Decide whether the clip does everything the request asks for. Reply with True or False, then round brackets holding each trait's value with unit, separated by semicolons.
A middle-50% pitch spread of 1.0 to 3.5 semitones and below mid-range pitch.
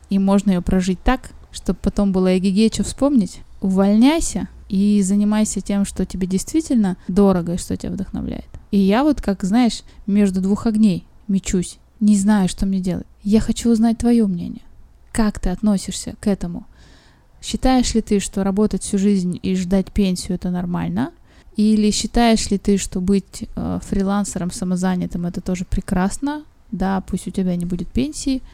False (2.6 semitones; 200 Hz)